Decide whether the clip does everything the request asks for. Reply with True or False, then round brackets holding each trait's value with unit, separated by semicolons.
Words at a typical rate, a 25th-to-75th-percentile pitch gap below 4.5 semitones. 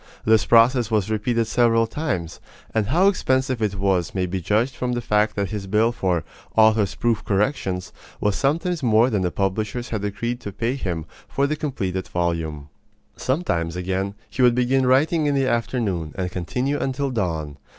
False (175 wpm; 5.1 semitones)